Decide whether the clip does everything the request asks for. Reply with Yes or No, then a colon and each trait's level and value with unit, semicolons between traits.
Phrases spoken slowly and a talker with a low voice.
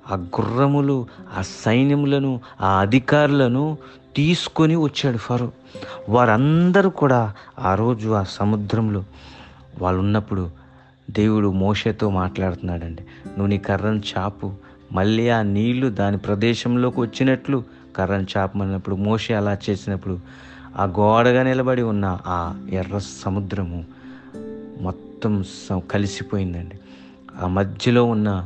Yes: slow, 105 wpm; low, 105 Hz